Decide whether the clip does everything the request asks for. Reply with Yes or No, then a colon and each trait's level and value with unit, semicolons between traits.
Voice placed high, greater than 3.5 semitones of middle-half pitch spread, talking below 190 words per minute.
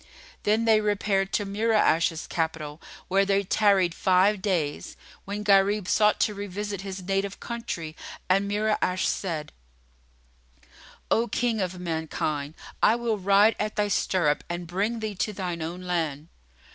No: high, 195 Hz; average, 3.2 semitones; average, 140 wpm